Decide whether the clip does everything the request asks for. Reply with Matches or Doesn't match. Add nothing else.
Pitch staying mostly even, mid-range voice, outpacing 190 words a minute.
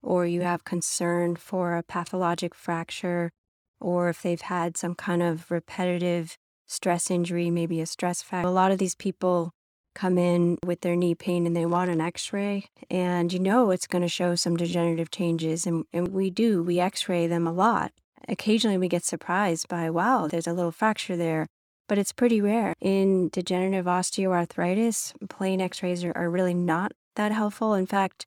Doesn't match